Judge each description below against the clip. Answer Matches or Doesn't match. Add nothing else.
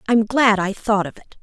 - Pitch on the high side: Matches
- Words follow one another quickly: Matches